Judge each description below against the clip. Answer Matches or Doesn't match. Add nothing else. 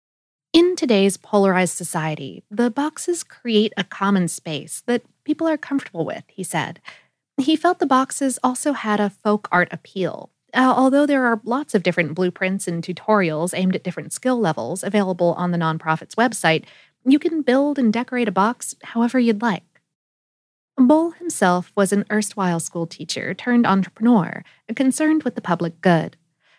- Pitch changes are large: Matches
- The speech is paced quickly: Doesn't match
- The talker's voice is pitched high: Matches